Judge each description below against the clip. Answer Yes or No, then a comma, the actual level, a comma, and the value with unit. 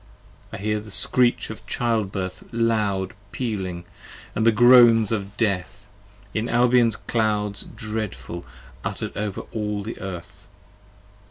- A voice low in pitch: Yes, low, 105 Hz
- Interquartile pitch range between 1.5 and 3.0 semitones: Yes, average, 2.7 semitones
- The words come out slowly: Yes, slow, 120 wpm